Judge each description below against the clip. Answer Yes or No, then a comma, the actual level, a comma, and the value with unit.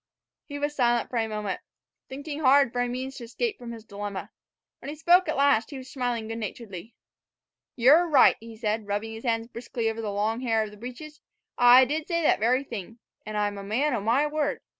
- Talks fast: Yes, fast, 220 wpm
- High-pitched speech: Yes, high, 240 Hz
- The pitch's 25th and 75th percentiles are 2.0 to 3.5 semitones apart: No, average, 4.2 semitones